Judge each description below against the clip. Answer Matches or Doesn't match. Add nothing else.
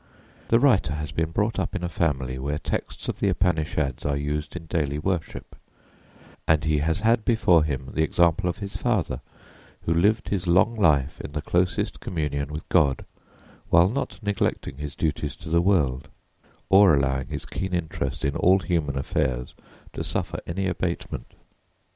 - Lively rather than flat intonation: Doesn't match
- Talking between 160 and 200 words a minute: Matches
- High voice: Doesn't match